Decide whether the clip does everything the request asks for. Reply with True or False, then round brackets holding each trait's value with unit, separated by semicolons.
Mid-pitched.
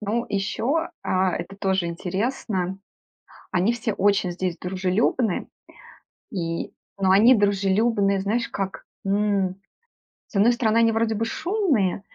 False (200 Hz)